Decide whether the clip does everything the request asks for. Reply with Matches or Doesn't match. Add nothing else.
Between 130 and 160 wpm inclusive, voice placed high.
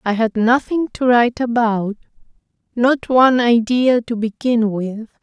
Matches